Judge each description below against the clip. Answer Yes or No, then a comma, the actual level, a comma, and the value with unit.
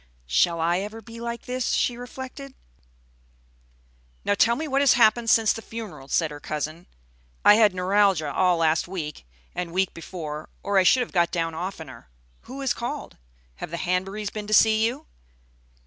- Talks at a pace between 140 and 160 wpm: No, average, 175 wpm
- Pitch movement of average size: No, wide, 5.7 semitones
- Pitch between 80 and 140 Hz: No, high, 195 Hz